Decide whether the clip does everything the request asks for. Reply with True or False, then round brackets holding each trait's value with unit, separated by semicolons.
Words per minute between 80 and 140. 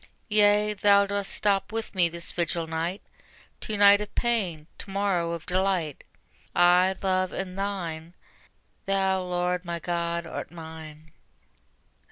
True (135 wpm)